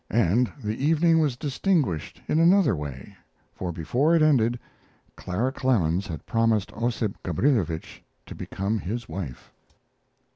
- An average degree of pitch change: No, wide, 7.6 semitones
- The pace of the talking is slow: Yes, slow, 125 wpm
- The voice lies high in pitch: No, low, 115 Hz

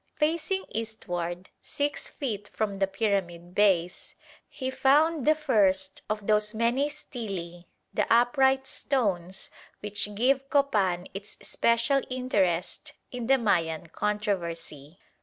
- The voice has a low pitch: No, high, 210 Hz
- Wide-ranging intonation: Yes, wide, 6.1 semitones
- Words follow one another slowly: Yes, slow, 115 wpm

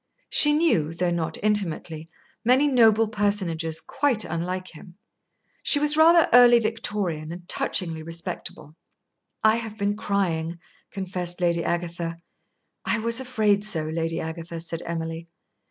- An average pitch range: Yes, average, 4.9 semitones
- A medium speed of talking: No, slow, 130 wpm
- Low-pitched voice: No, medium, 180 Hz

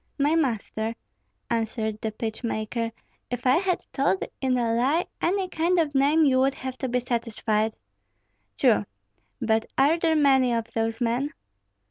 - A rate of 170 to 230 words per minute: No, average, 155 wpm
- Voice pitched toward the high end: Yes, very high, 250 Hz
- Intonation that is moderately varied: Yes, average, 4.2 semitones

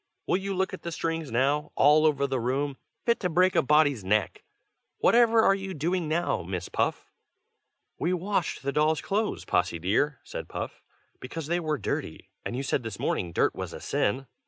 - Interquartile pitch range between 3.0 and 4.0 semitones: No, average, 5.3 semitones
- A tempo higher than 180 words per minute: Yes, average, 190 wpm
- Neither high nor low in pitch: Yes, medium, 150 Hz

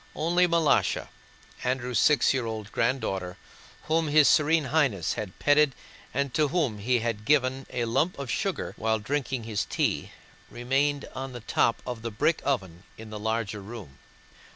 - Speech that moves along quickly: No, average, 160 wpm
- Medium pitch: No, low, 125 Hz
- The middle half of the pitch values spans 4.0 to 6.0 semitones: Yes, average, 4.7 semitones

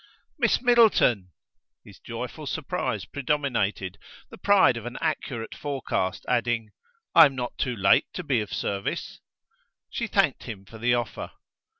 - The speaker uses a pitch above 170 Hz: No, low, 120 Hz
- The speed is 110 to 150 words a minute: Yes, average, 140 wpm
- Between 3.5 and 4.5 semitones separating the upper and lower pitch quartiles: No, average, 5.2 semitones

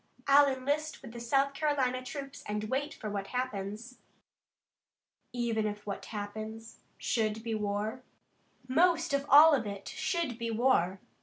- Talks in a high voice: Yes, high, 240 Hz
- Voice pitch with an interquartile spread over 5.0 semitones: No, average, 4.5 semitones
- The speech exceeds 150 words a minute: No, average, 145 wpm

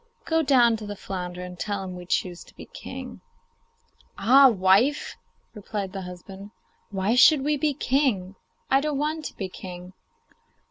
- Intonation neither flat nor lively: No, wide, 6.5 semitones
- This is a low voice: No, high, 205 Hz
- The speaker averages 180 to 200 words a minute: No, average, 160 wpm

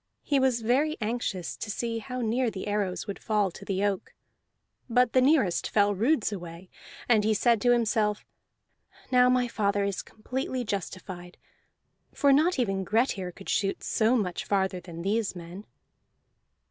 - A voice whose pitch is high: Yes, high, 210 Hz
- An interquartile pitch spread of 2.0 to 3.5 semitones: No, average, 4.1 semitones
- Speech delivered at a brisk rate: No, average, 160 wpm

